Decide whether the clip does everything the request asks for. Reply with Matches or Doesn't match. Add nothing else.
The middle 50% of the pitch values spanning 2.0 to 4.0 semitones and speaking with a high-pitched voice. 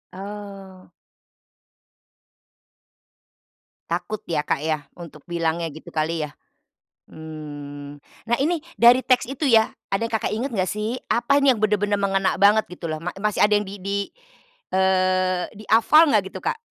Doesn't match